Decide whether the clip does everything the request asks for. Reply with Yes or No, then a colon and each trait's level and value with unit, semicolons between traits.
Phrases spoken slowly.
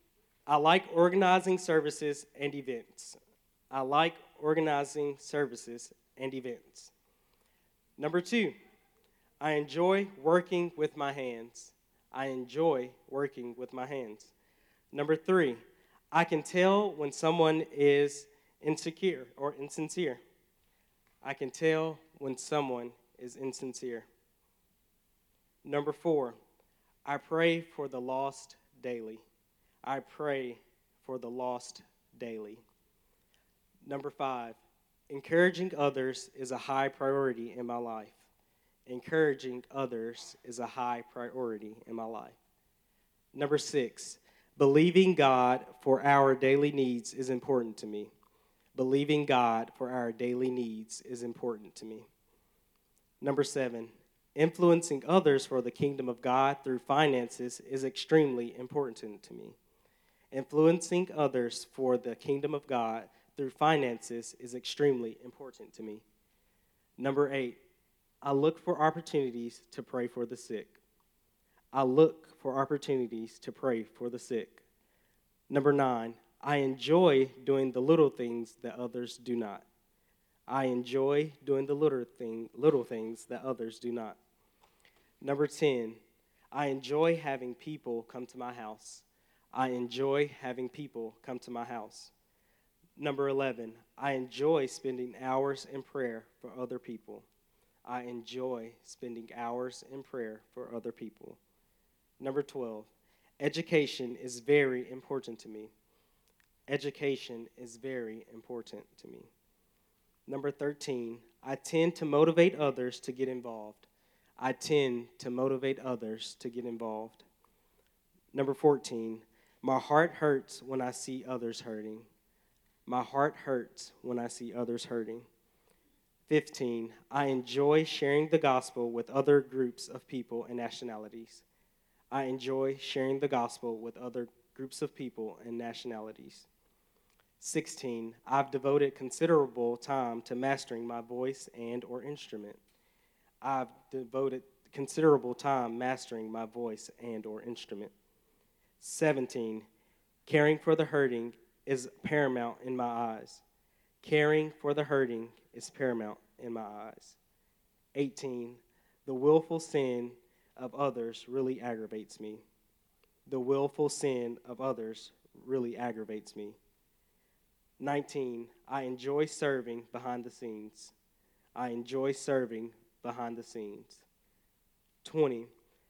Yes: slow, 120 wpm